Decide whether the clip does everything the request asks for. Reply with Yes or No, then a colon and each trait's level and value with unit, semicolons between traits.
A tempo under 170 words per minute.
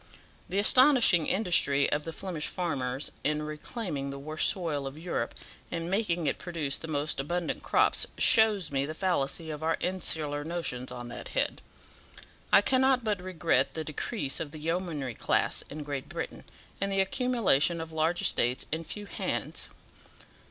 Yes: average, 160 wpm